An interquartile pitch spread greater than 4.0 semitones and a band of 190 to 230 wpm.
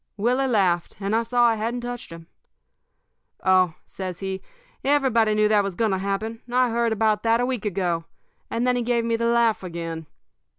No: average, 3.7 semitones; average, 195 wpm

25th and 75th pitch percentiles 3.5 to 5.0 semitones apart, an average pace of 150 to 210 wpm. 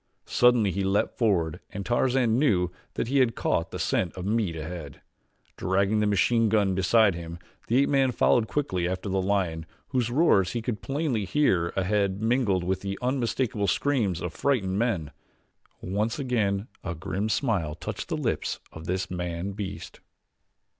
Yes: average, 4.5 semitones; average, 165 wpm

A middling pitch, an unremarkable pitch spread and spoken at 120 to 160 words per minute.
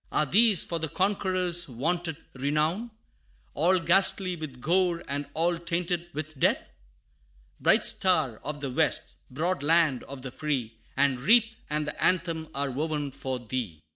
Yes: medium, 160 Hz; average, 4.1 semitones; average, 150 wpm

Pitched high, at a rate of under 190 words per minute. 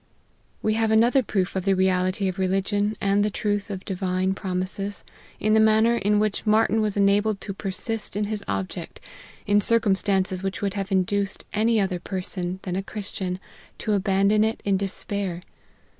Yes: high, 200 Hz; average, 175 wpm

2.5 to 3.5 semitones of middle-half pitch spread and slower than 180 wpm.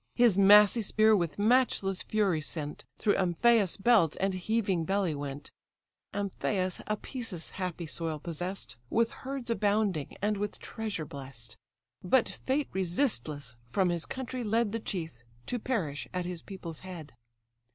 No: average, 4.9 semitones; average, 140 wpm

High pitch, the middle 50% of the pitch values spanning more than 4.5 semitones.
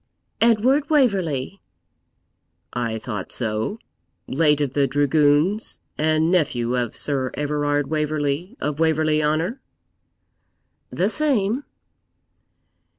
No: medium, 150 Hz; average, 5.1 semitones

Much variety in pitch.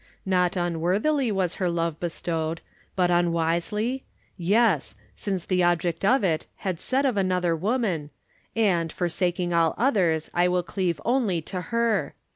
No: average, 3.6 semitones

